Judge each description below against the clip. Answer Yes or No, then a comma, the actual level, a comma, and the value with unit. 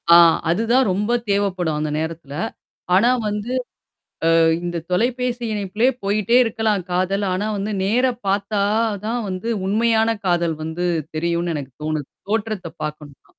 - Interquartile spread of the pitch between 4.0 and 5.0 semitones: Yes, average, 4.6 semitones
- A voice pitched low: No, high, 195 Hz